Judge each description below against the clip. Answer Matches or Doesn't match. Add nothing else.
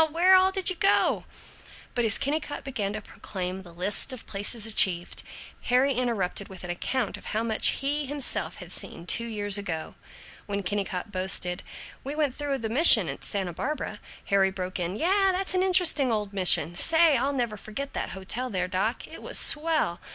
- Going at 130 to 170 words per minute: Doesn't match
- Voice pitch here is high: Matches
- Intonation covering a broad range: Matches